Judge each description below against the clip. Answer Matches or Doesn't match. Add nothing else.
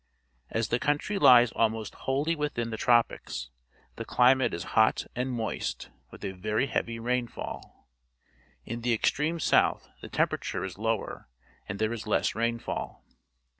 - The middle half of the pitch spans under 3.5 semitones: Matches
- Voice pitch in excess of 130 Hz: Doesn't match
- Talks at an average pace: Matches